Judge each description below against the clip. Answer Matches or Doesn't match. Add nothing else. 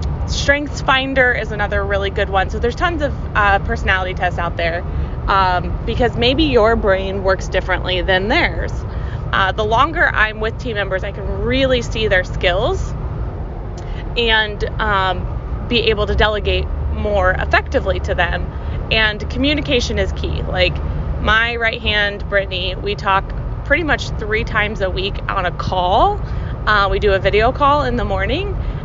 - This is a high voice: Matches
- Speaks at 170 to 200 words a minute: Doesn't match